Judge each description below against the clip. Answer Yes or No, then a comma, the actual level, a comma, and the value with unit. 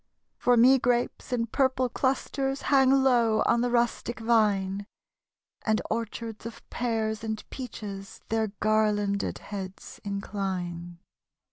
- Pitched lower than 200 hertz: No, high, 225 Hz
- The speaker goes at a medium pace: No, slow, 115 wpm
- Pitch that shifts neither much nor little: Yes, average, 3.3 semitones